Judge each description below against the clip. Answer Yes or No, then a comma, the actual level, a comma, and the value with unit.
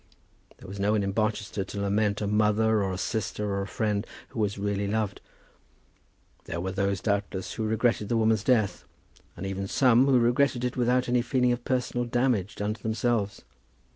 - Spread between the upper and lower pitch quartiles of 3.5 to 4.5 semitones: No, average, 3.1 semitones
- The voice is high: No, low, 110 Hz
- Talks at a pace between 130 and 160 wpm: No, average, 190 wpm